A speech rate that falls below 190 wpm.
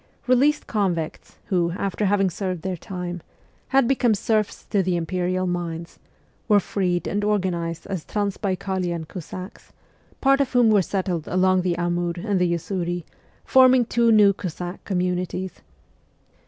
Yes: average, 140 wpm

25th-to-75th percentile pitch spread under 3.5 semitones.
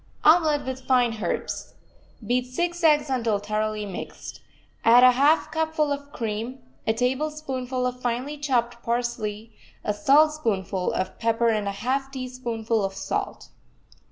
No: average, 4.2 semitones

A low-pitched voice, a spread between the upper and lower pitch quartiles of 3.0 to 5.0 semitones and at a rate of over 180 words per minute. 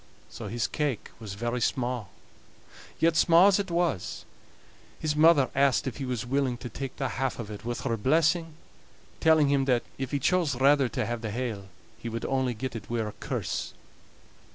Yes: low, 130 Hz; average, 4.0 semitones; average, 190 wpm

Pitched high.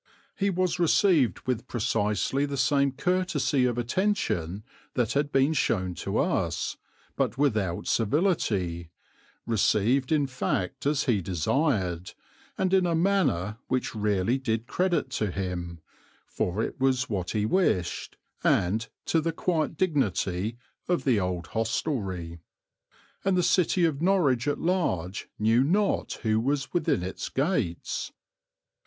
No: low, 125 Hz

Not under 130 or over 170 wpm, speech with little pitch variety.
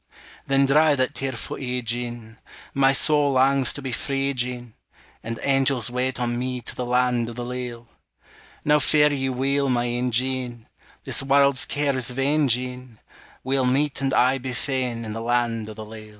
No: average, 180 wpm; narrow, 2.1 semitones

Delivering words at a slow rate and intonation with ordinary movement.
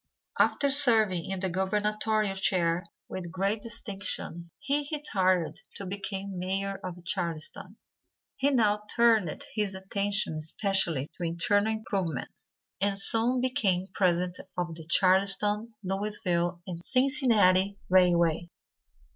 Yes: slow, 115 wpm; average, 3.1 semitones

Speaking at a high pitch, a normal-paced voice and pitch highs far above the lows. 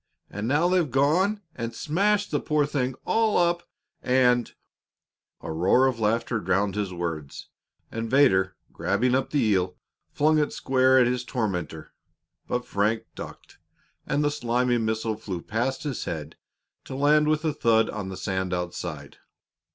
No: low, 120 Hz; average, 160 wpm; wide, 6.3 semitones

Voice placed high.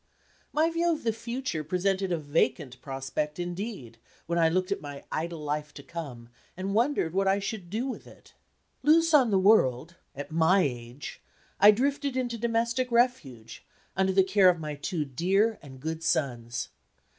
No: medium, 180 Hz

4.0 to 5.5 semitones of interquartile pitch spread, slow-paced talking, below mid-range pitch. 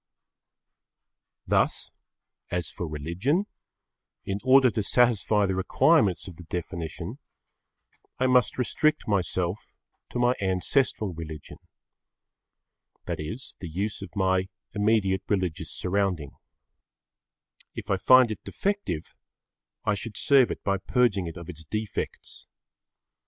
Yes: average, 5.0 semitones; slow, 115 wpm; low, 100 Hz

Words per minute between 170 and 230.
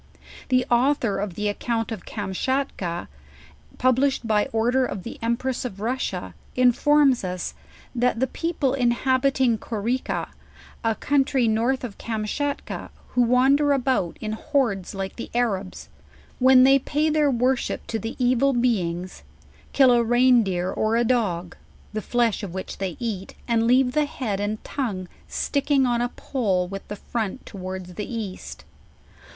No: average, 155 wpm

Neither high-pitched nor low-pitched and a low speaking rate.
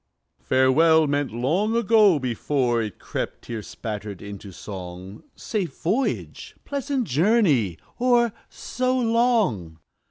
Yes: medium, 145 Hz; slow, 105 wpm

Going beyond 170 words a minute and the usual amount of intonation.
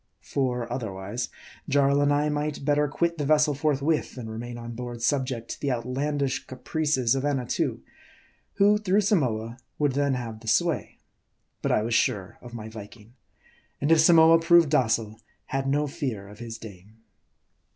No: average, 165 wpm; average, 4.3 semitones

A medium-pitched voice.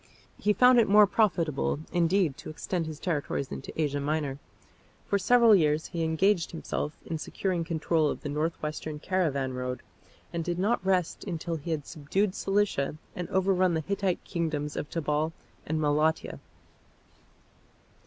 Yes: medium, 165 Hz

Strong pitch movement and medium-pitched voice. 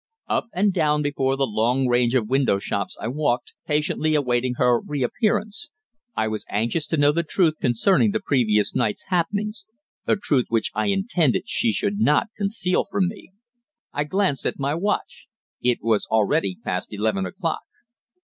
Yes: wide, 8.1 semitones; medium, 145 Hz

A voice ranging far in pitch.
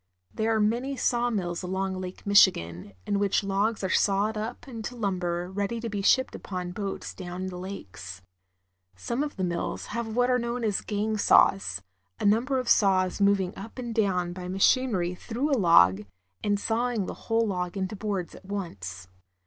No: average, 3.9 semitones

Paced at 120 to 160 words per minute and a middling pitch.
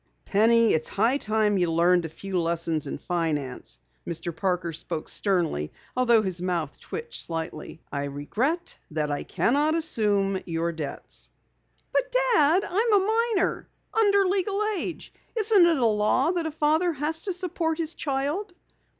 No: average, 150 wpm; high, 220 Hz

